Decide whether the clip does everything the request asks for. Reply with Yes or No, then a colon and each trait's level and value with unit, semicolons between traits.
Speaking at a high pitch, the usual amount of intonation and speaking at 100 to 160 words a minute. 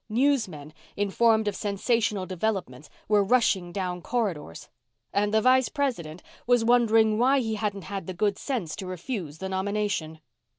Yes: high, 205 Hz; average, 4.0 semitones; average, 145 wpm